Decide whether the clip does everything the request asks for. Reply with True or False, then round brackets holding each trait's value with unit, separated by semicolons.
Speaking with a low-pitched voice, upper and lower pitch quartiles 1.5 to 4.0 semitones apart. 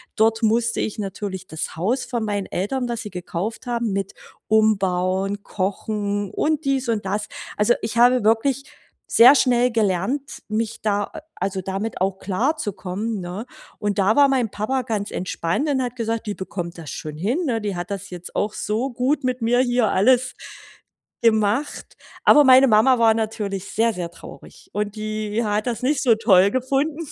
False (220 Hz; 3.7 semitones)